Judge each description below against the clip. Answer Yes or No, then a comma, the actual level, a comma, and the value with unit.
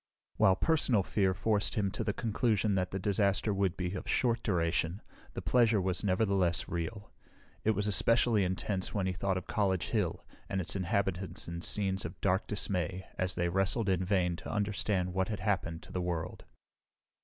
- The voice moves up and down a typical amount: No, narrow, 2.3 semitones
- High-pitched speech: No, very low, 95 Hz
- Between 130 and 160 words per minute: No, average, 180 wpm